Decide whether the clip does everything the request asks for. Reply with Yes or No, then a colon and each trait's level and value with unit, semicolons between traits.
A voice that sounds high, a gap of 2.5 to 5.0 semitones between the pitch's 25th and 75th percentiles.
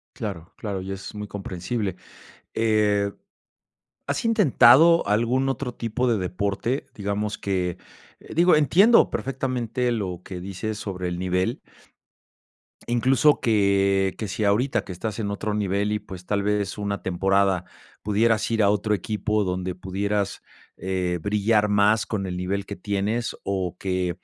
No: low, 100 Hz; average, 2.9 semitones